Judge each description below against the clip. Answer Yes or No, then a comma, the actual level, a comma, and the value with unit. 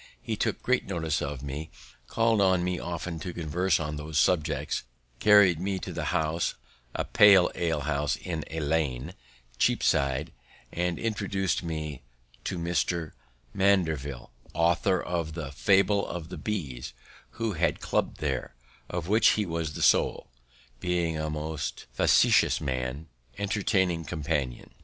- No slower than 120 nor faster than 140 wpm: Yes, slow, 135 wpm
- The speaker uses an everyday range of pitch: Yes, average, 3.5 semitones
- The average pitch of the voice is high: No, very low, 85 Hz